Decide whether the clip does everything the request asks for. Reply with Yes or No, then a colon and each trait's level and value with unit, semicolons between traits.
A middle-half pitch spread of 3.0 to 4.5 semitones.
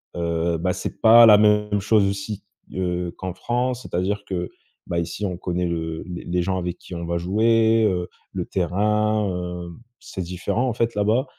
Yes: average, 3.4 semitones